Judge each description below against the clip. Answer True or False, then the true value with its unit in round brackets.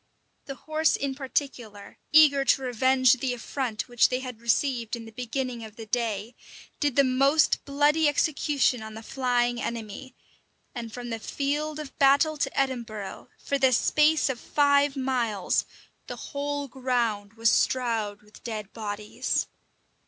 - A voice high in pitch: True (255 Hz)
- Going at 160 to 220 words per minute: False (150 wpm)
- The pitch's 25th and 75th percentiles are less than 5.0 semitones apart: True (3.6 semitones)